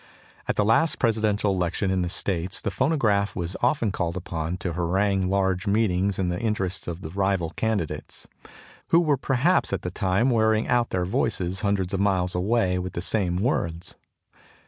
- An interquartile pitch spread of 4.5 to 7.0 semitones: No, average, 3.6 semitones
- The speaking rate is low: No, average, 175 wpm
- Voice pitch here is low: Yes, very low, 95 Hz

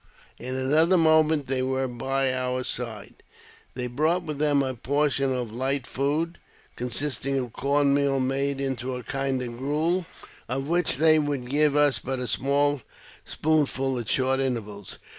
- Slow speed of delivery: No, average, 160 wpm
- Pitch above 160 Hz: No, low, 135 Hz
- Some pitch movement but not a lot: No, narrow, 2.3 semitones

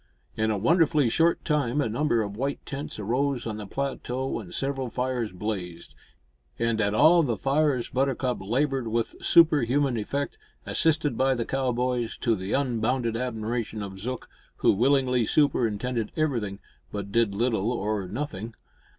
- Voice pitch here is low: Yes, low, 120 Hz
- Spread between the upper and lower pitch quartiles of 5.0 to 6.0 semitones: No, average, 4.0 semitones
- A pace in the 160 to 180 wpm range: No, average, 150 wpm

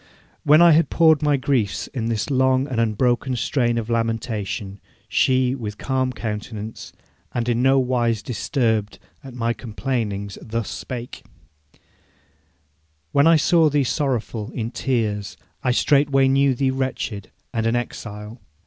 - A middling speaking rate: Yes, average, 145 wpm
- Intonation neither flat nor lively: Yes, average, 3.2 semitones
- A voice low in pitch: Yes, low, 120 Hz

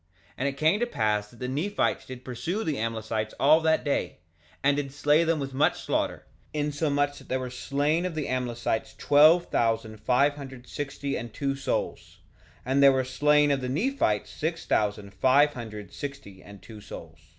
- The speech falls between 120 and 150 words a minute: No, average, 185 wpm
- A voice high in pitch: No, low, 135 Hz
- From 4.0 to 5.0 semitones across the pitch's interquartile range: Yes, average, 4.3 semitones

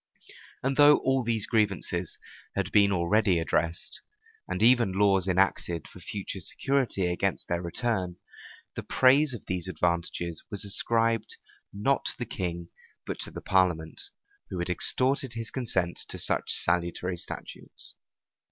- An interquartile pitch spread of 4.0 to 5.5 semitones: Yes, average, 4.9 semitones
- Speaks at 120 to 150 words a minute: Yes, average, 140 wpm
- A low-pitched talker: Yes, very low, 95 Hz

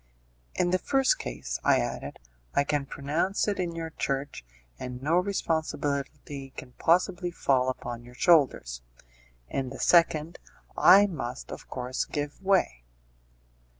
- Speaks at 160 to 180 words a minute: No, slow, 135 wpm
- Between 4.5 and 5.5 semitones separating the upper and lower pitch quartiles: Yes, average, 5.2 semitones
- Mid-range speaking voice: Yes, medium, 145 Hz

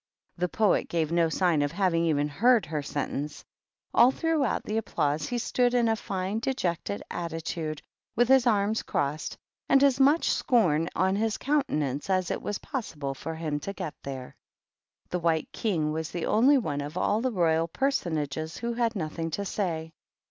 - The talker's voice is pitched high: No, medium, 175 Hz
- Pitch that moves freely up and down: Yes, wide, 6.5 semitones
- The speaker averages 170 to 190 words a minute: Yes, average, 175 wpm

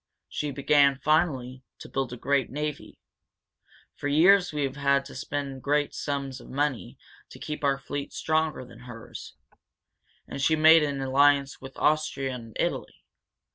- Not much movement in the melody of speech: Yes, narrow, 2.0 semitones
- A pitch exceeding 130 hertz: Yes, medium, 140 Hz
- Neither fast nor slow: Yes, average, 155 wpm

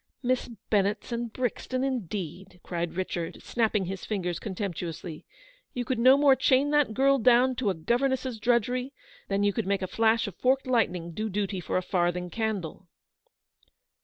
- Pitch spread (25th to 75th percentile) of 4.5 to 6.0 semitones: Yes, wide, 5.5 semitones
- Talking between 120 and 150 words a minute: No, average, 175 wpm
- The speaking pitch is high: Yes, high, 220 Hz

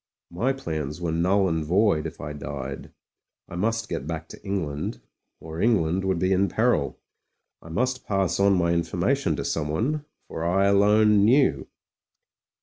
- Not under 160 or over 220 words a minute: Yes, average, 175 wpm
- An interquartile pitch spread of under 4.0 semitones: No, average, 4.5 semitones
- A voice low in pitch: Yes, very low, 95 Hz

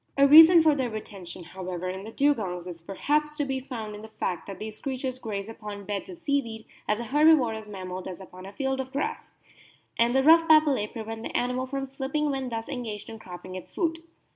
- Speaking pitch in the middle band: No, high, 230 Hz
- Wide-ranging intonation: Yes, wide, 5.7 semitones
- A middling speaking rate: No, fast, 215 wpm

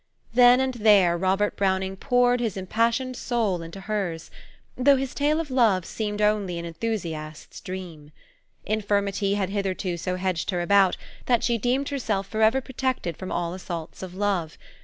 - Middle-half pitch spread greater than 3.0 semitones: Yes, average, 4.5 semitones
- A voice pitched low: No, high, 200 Hz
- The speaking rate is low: No, average, 160 wpm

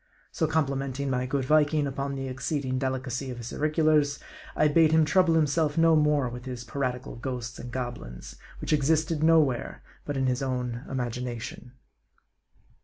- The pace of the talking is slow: No, average, 160 wpm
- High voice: No, low, 135 Hz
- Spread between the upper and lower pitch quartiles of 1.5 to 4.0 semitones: Yes, average, 3.3 semitones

